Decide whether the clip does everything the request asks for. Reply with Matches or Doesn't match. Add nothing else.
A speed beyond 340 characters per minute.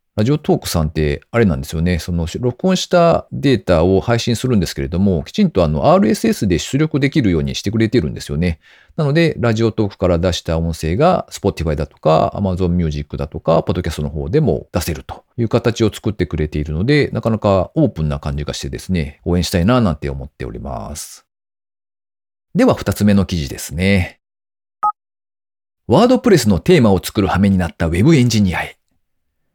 Matches